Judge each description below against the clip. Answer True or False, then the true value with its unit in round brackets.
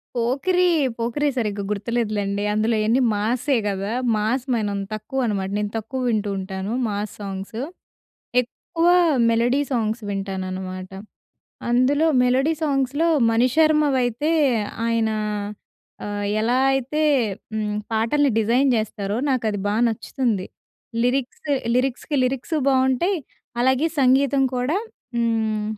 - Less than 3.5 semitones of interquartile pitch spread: False (4.2 semitones)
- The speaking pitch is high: True (235 Hz)